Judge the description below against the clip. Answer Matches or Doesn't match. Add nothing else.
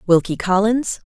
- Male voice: Doesn't match